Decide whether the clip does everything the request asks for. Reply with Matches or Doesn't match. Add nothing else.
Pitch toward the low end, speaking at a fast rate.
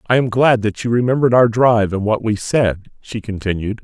Matches